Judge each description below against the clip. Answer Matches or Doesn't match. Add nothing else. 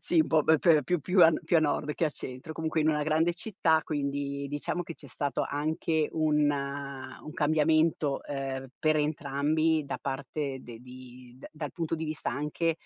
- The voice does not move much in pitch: Matches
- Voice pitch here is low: Doesn't match